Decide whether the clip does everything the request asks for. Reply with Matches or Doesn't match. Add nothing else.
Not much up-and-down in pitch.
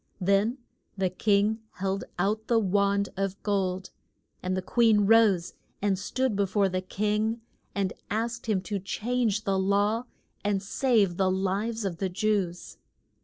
Matches